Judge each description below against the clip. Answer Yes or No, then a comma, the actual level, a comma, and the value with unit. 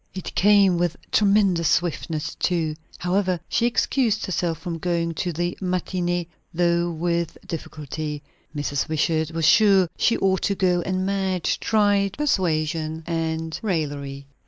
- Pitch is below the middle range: No, medium, 175 Hz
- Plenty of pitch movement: No, average, 3.0 semitones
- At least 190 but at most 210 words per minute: No, slow, 135 wpm